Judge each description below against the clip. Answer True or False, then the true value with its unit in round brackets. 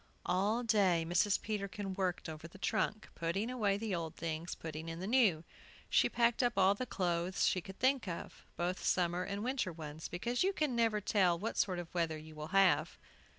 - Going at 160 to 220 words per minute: True (195 wpm)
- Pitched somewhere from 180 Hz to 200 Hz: True (190 Hz)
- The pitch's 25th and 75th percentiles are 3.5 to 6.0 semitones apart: True (4.3 semitones)